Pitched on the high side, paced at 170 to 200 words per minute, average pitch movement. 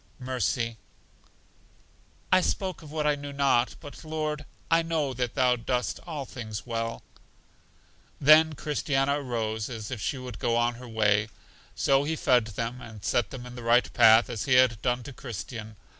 No: low, 125 Hz; average, 175 wpm; average, 3.8 semitones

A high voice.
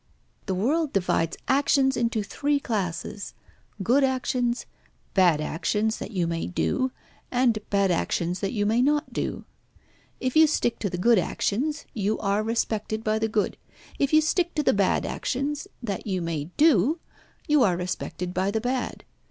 Yes: high, 220 Hz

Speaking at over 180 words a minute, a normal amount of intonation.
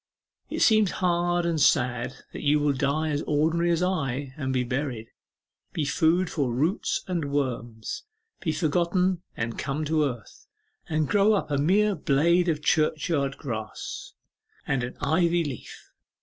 No: average, 150 wpm; average, 3.9 semitones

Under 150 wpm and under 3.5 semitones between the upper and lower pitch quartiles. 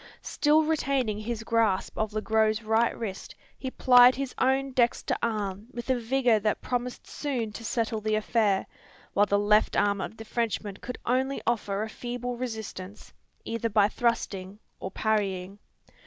No: average, 160 wpm; average, 2.8 semitones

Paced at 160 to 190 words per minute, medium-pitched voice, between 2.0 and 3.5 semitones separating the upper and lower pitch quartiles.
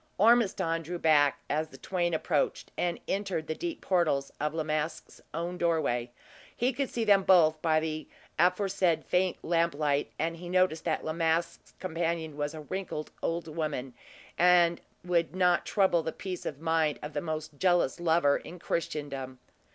Yes: average, 165 wpm; medium, 165 Hz; narrow, 2.5 semitones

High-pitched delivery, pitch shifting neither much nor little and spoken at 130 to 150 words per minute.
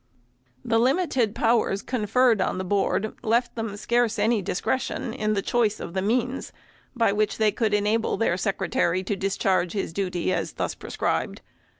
No: high, 215 Hz; average, 3.0 semitones; average, 165 wpm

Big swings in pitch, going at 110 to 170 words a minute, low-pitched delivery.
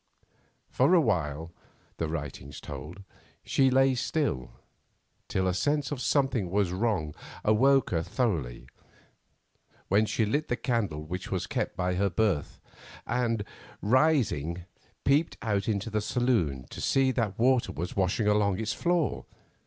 Yes: wide, 6.6 semitones; average, 140 wpm; low, 105 Hz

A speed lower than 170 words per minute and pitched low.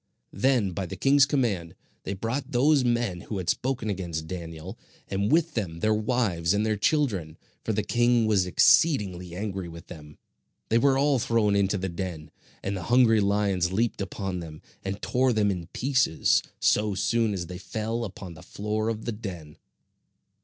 No: average, 175 wpm; low, 105 Hz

